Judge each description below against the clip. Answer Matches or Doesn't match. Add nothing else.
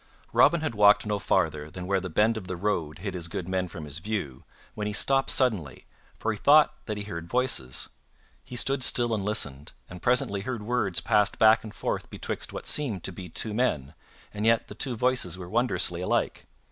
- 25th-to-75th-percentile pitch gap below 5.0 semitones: Matches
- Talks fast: Matches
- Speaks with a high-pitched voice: Doesn't match